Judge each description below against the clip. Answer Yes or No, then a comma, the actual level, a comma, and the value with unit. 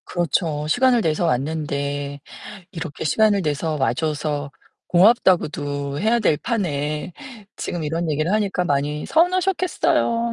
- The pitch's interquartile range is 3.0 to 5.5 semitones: No, wide, 5.9 semitones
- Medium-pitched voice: Yes, medium, 160 Hz